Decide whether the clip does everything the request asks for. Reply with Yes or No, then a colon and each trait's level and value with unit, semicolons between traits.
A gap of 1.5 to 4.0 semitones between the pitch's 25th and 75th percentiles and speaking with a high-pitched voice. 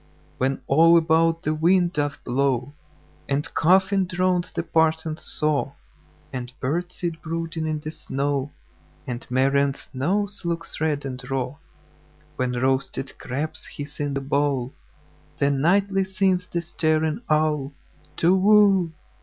No: average, 3.5 semitones; medium, 155 Hz